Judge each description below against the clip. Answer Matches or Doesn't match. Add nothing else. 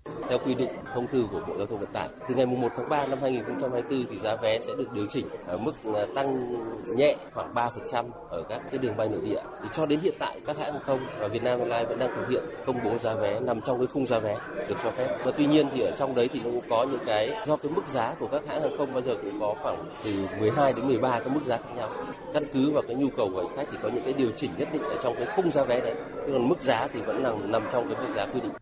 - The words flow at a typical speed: Doesn't match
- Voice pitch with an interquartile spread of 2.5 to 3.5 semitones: Matches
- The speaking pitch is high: Doesn't match